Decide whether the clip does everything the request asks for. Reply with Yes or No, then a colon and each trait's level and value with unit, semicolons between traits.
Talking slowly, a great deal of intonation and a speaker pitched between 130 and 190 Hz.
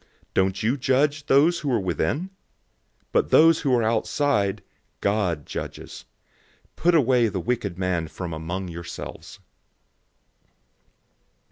No: slow, 120 wpm; wide, 7.4 semitones; low, 110 Hz